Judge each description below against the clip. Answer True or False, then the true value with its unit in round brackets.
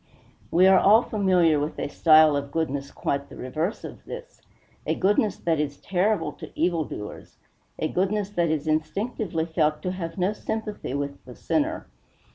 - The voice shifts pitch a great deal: False (4.8 semitones)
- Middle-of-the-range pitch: True (170 Hz)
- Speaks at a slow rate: False (170 wpm)